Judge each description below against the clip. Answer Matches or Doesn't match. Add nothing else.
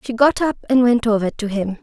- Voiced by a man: Doesn't match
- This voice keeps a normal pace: Doesn't match